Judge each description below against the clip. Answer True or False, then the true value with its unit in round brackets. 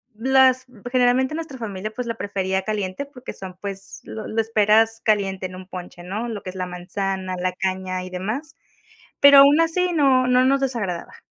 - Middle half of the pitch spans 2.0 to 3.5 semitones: False (5.4 semitones)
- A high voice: True (215 Hz)